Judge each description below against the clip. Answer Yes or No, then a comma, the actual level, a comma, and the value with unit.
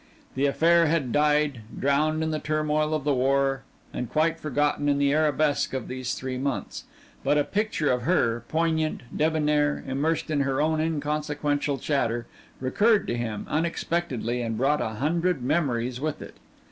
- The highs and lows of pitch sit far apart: No, average, 2.9 semitones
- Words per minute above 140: Yes, average, 160 wpm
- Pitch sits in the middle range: Yes, medium, 145 Hz